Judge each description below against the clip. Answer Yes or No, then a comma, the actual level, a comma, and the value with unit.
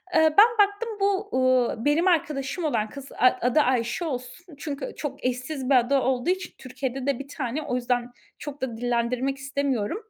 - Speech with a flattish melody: No, average, 3.8 semitones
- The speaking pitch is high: Yes, very high, 270 Hz